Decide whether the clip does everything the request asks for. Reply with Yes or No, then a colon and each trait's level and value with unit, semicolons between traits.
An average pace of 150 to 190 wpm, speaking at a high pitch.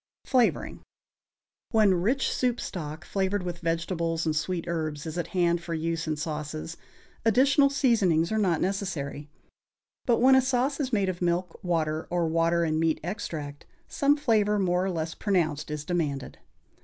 No: average, 160 wpm; medium, 175 Hz